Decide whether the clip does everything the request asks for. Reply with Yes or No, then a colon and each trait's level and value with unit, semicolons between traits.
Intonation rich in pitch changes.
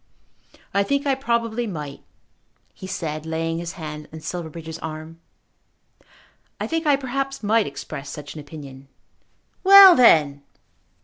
Yes: wide, 8.0 semitones